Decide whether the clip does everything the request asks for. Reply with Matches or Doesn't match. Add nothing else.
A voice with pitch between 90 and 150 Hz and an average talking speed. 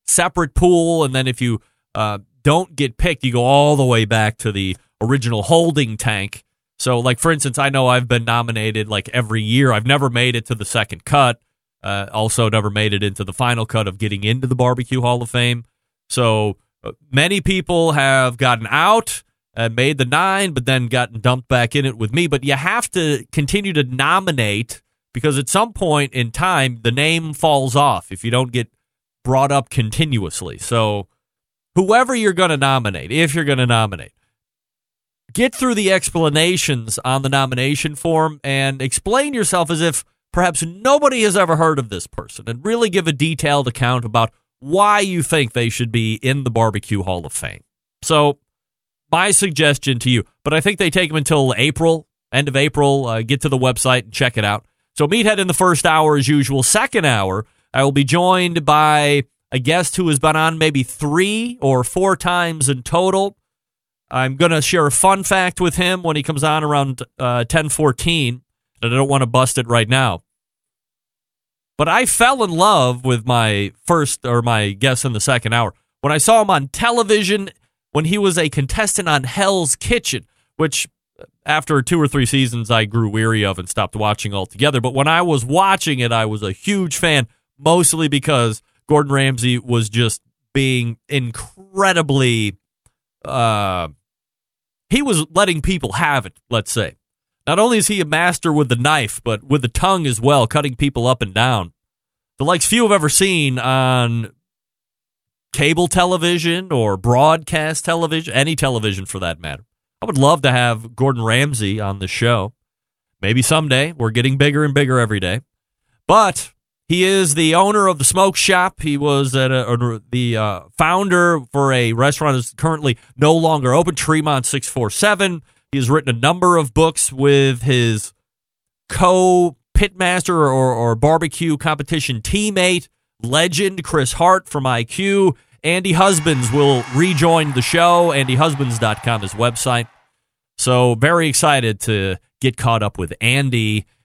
Matches